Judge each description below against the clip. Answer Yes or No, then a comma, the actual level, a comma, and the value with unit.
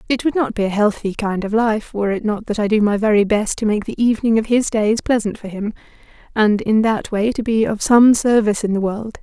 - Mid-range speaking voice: No, high, 215 Hz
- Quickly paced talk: Yes, fast, 260 wpm